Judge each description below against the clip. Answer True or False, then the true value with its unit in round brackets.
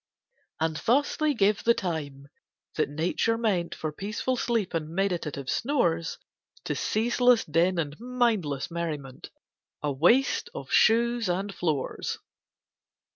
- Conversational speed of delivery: False (125 wpm)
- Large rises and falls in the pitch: True (6.7 semitones)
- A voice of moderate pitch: True (180 Hz)